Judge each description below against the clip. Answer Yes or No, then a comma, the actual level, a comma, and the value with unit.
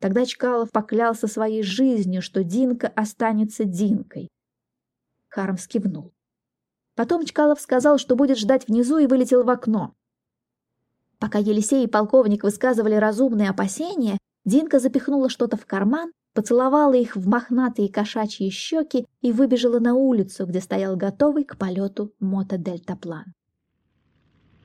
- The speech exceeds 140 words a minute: No, average, 120 wpm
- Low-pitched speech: No, high, 220 Hz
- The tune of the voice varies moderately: Yes, average, 4.4 semitones